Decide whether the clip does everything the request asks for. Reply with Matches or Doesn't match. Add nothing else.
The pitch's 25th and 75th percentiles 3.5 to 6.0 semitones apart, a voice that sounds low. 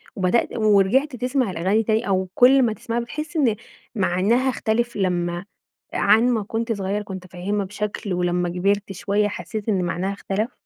Doesn't match